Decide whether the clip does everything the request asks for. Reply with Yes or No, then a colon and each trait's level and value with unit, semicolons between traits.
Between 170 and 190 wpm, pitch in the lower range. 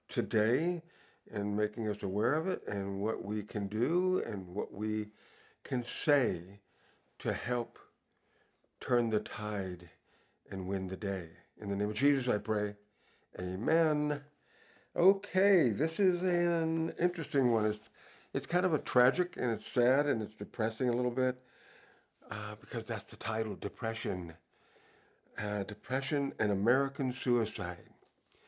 No: average, 140 wpm; low, 110 Hz